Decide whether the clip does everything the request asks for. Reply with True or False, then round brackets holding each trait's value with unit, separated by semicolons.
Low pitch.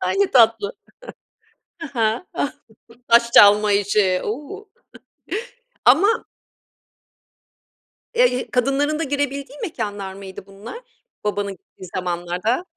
False (225 Hz)